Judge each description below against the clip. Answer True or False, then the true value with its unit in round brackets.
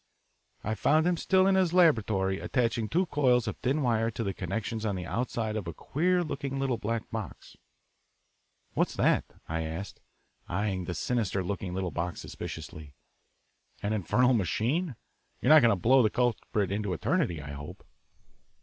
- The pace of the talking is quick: False (165 wpm)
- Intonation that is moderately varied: False (5.7 semitones)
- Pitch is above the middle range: False (110 Hz)